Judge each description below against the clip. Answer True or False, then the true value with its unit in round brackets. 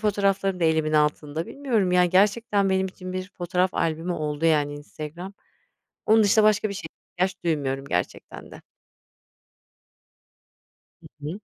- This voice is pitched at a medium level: True (180 Hz)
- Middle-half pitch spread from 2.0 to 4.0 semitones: False (4.4 semitones)